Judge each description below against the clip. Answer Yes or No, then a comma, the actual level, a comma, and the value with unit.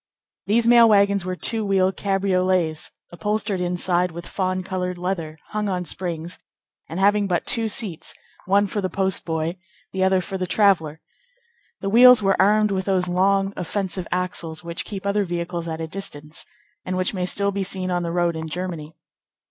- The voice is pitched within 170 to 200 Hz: Yes, medium, 185 Hz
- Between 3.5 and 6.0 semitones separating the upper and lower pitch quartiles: No, narrow, 2.4 semitones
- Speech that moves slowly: No, average, 175 wpm